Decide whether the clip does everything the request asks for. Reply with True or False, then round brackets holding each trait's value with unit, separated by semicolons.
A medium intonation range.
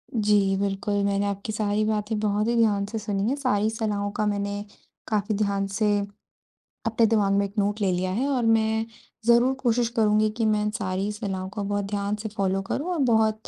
False (1.7 semitones)